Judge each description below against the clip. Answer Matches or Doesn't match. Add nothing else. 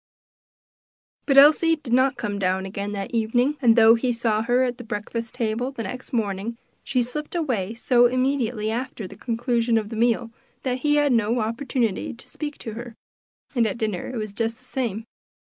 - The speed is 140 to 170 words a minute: Doesn't match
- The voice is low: Doesn't match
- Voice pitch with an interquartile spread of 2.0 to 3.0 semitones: Matches